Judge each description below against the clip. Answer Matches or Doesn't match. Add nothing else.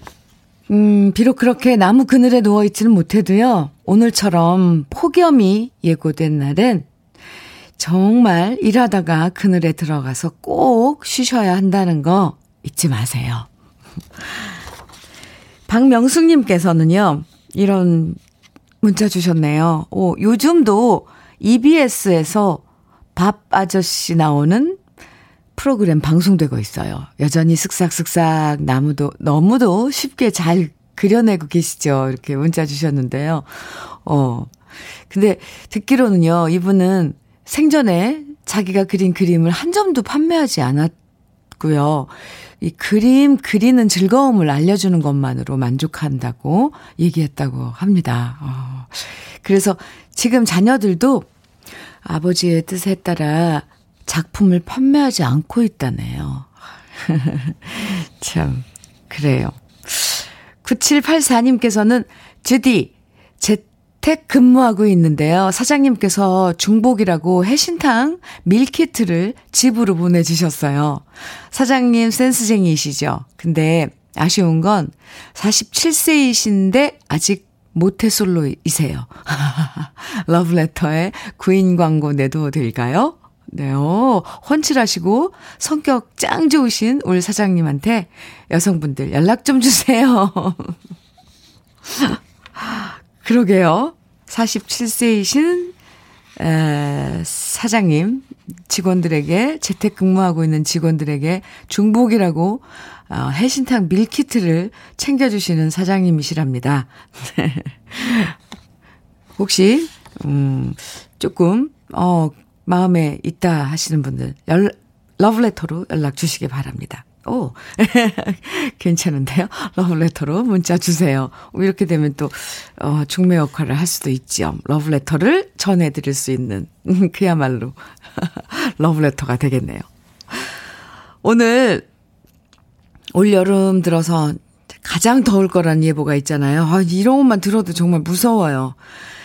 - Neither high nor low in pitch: Matches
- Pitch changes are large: Matches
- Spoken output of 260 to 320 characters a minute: Doesn't match